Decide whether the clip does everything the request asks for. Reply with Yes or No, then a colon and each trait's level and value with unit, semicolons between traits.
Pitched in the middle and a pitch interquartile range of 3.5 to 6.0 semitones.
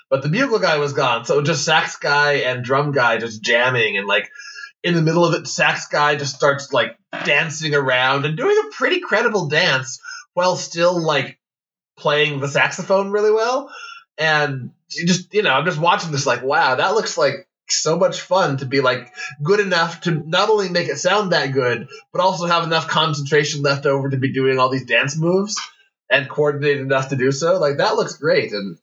Yes: medium, 160 Hz; average, 5.2 semitones